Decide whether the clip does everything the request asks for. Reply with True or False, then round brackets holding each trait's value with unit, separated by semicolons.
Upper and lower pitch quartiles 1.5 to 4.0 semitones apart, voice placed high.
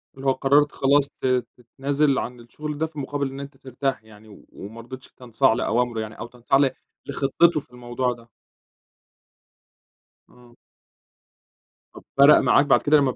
False (2.8 semitones; 130 Hz)